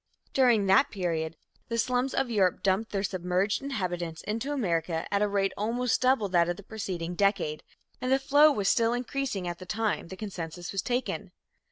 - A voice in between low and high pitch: No, high, 200 Hz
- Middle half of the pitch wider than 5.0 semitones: Yes, wide, 5.4 semitones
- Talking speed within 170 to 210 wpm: Yes, average, 185 wpm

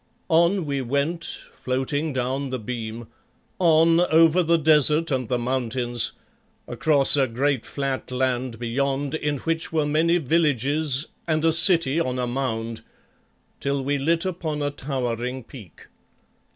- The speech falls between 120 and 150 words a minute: Yes, average, 140 wpm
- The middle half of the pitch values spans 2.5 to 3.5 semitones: No, average, 3.9 semitones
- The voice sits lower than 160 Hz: Yes, medium, 140 Hz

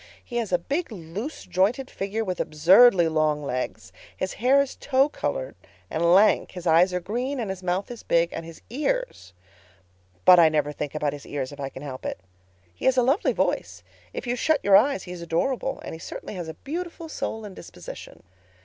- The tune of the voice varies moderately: No, wide, 8.2 semitones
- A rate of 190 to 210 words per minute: Yes, average, 195 wpm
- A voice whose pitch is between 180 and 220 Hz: Yes, medium, 185 Hz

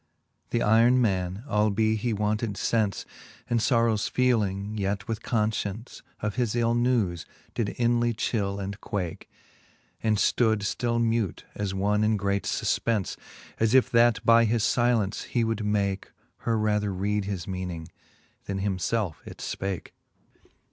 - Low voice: Yes, low, 105 Hz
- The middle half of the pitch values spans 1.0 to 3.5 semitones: Yes, average, 2.8 semitones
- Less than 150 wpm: Yes, average, 140 wpm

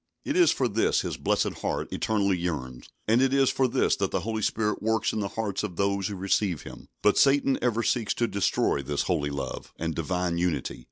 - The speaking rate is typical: No, fast, 215 wpm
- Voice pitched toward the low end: Yes, low, 100 Hz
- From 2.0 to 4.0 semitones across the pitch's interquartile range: No, average, 4.6 semitones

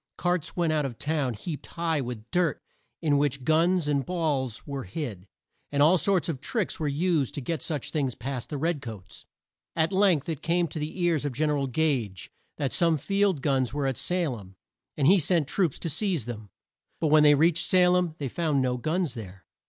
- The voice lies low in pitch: No, medium, 150 Hz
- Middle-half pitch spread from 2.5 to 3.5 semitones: No, average, 4.2 semitones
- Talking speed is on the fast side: Yes, fast, 215 wpm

